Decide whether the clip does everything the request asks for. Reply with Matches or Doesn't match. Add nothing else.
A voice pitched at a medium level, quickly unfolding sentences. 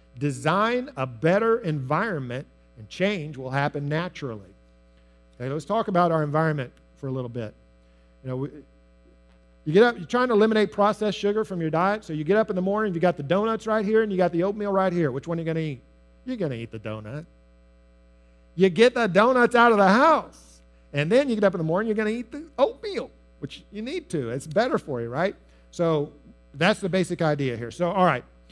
Matches